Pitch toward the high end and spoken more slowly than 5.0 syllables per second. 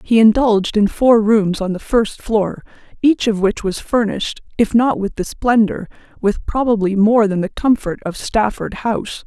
Yes: high, 220 Hz; 4.6 syllables/s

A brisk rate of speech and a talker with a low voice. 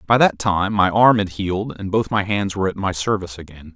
Yes: fast, 255 wpm; very low, 95 Hz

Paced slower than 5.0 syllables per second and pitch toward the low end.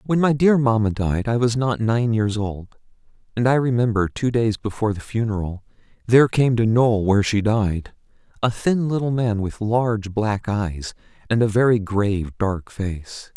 Yes: 4.7 syllables/s; low, 110 Hz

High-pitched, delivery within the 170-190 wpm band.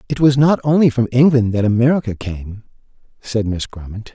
No: low, 120 Hz; average, 175 wpm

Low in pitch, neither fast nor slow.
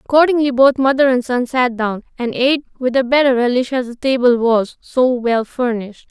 No: very high, 250 Hz; average, 195 wpm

